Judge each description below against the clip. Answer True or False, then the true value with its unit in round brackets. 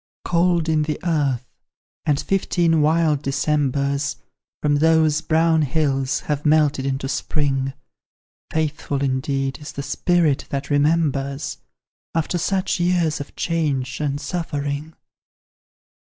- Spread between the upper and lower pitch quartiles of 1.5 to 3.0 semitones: True (2.6 semitones)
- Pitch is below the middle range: False (150 Hz)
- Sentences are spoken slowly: True (110 wpm)